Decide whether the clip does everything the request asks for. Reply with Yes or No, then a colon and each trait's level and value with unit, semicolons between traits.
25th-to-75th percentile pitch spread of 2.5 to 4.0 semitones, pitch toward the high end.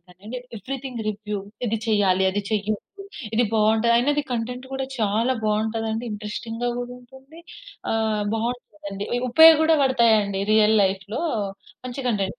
Yes: average, 2.8 semitones; high, 225 Hz